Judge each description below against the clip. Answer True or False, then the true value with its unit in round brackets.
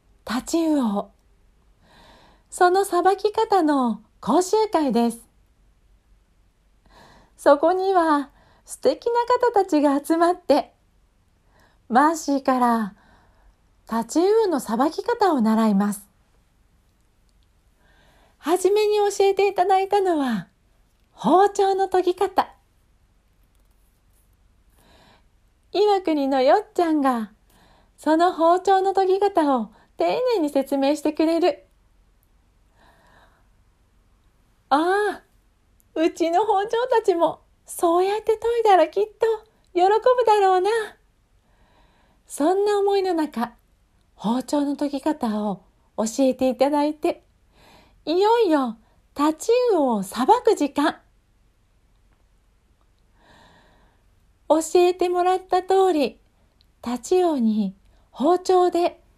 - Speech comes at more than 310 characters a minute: False (180 characters per minute)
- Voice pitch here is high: True (305 Hz)